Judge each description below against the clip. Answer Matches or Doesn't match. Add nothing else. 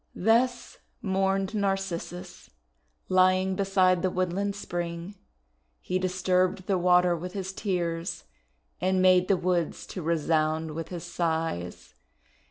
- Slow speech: Matches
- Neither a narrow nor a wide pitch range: Doesn't match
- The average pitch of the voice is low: Doesn't match